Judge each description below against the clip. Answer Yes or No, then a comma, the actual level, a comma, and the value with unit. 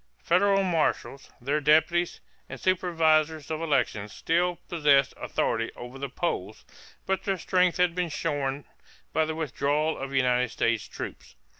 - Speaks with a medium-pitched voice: Yes, medium, 155 Hz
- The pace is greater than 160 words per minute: No, average, 140 wpm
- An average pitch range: Yes, average, 4.1 semitones